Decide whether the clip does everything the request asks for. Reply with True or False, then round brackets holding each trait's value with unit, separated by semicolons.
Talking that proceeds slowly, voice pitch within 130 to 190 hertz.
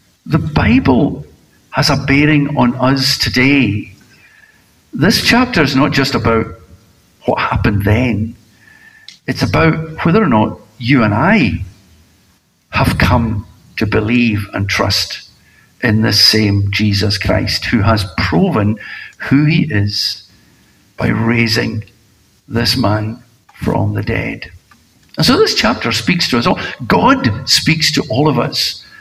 False (130 wpm; 115 Hz)